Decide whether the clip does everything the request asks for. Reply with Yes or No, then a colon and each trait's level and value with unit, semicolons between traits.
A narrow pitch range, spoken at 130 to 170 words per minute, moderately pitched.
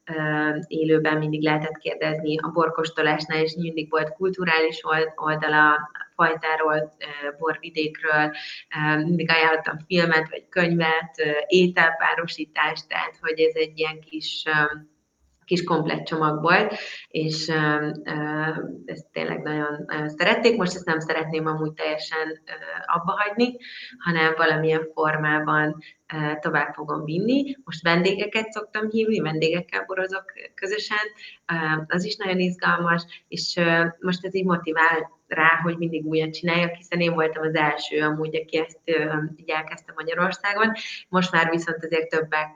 No: narrow, 2.0 semitones; average, 120 wpm; medium, 160 Hz